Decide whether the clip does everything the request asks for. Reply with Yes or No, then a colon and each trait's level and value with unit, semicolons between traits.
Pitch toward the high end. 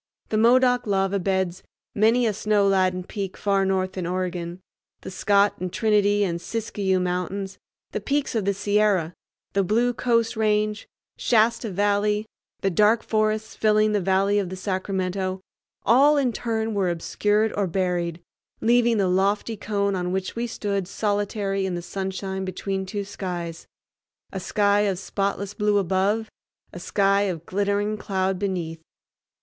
Yes: high, 200 Hz